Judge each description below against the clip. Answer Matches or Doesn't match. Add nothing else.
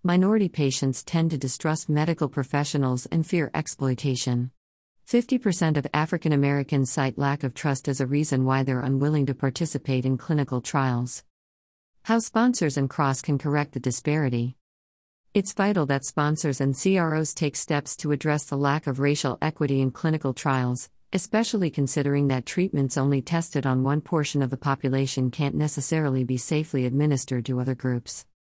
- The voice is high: Doesn't match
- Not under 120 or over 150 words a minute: Doesn't match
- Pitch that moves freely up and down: Doesn't match